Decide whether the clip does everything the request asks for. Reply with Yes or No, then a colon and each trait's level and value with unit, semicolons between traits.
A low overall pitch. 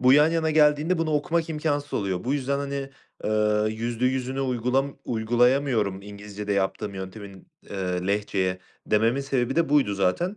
Yes: low, 125 Hz